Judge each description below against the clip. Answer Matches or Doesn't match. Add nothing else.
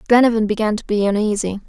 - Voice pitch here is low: Doesn't match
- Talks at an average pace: Matches